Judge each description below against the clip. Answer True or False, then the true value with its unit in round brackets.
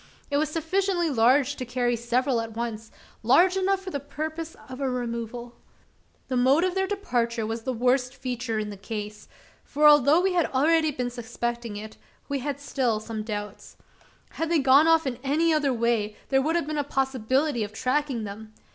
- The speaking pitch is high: True (260 Hz)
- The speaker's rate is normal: True (190 wpm)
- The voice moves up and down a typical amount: True (4.5 semitones)